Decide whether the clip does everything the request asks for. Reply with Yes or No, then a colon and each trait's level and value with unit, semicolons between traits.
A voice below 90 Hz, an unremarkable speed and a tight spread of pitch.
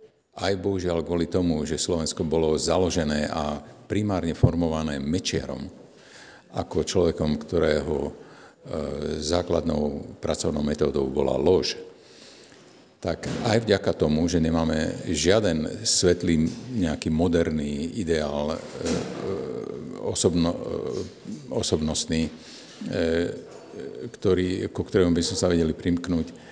No: very low, 80 Hz; slow, 90 wpm; narrow, 2.1 semitones